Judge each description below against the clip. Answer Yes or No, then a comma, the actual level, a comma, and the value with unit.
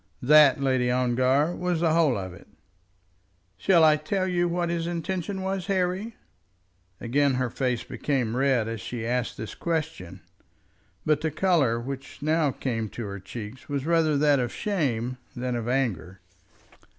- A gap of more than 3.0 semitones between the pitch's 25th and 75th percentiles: Yes, wide, 5.6 semitones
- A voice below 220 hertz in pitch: Yes, medium, 140 Hz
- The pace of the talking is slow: No, average, 155 wpm